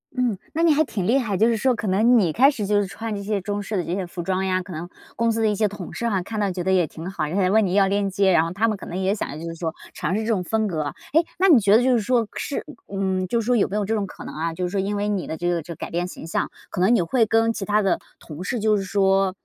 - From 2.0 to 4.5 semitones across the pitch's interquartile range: Yes, average, 3.2 semitones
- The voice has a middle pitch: No, high, 200 Hz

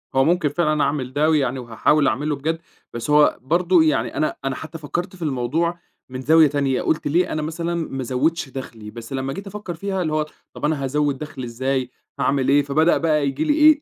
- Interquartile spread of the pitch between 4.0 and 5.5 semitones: No, average, 3.6 semitones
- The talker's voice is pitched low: No, medium, 150 Hz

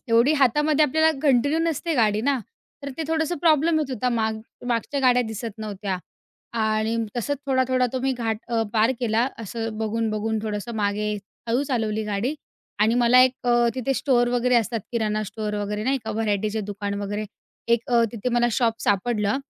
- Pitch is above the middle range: Yes, high, 235 Hz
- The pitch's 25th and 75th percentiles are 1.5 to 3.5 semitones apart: Yes, average, 3.1 semitones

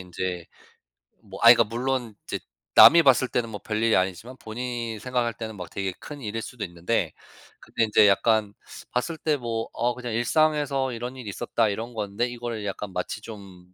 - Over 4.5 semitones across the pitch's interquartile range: No, average, 3.2 semitones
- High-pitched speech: No, low, 115 Hz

